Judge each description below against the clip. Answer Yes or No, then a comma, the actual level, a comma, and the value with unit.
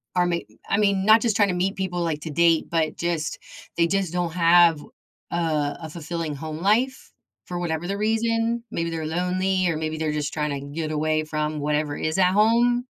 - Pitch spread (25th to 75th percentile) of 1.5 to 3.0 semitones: No, average, 3.7 semitones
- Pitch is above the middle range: No, medium, 170 Hz